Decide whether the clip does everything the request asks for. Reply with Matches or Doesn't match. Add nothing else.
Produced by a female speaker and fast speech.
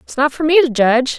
Matches